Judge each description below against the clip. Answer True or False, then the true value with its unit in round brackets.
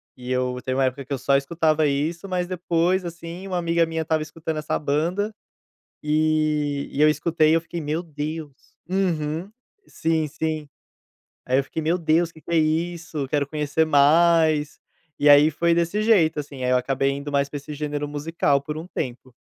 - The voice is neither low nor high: True (155 Hz)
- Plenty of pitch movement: False (2.6 semitones)